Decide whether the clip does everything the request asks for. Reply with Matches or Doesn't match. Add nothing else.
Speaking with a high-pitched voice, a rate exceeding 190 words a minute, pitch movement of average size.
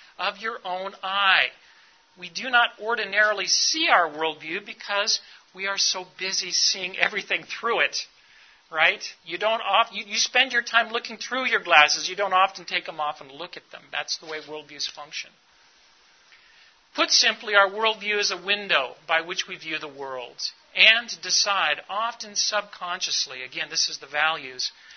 Doesn't match